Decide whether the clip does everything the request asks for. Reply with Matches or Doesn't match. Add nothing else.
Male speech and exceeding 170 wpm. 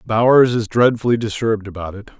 Doesn't match